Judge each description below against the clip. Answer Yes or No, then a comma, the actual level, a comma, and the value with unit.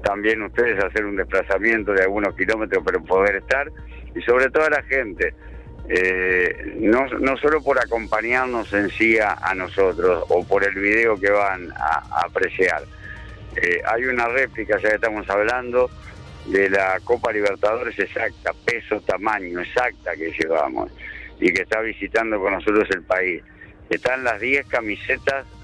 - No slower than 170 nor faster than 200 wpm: No, average, 155 wpm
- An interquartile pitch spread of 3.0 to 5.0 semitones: Yes, average, 4.1 semitones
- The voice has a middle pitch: No, low, 110 Hz